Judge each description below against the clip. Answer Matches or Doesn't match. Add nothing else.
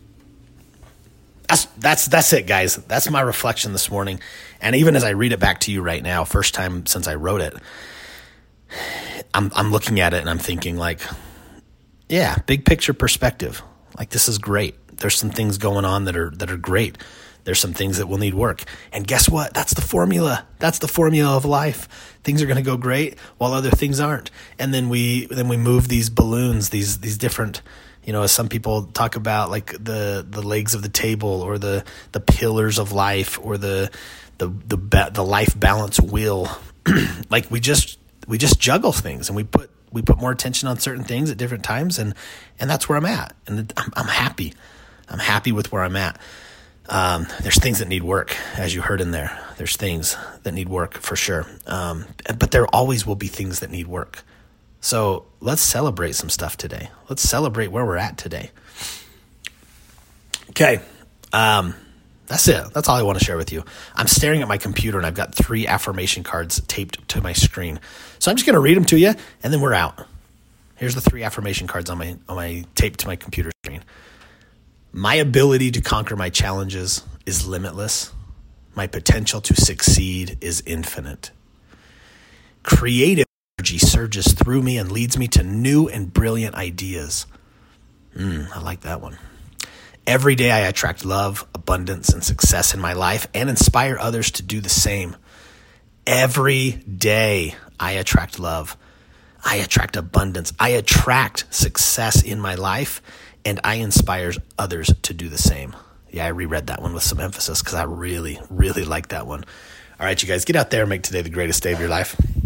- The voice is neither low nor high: Doesn't match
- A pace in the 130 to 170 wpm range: Doesn't match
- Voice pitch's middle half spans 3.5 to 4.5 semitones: Matches